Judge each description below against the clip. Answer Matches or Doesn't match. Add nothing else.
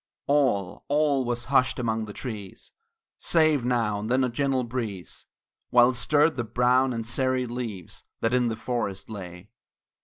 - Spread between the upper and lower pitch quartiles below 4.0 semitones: Matches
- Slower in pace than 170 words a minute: Matches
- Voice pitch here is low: Matches